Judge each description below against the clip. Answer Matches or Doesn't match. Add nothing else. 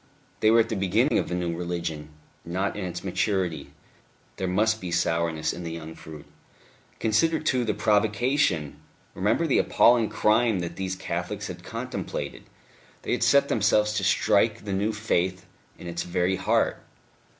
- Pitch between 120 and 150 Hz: Doesn't match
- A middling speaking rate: Matches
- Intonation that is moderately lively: Matches